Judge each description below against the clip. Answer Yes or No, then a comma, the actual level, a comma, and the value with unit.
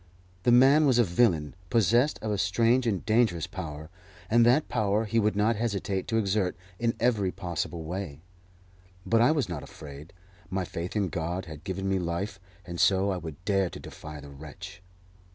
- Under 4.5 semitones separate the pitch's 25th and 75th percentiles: No, average, 4.9 semitones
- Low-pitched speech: Yes, very low, 95 Hz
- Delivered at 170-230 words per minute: Yes, average, 185 wpm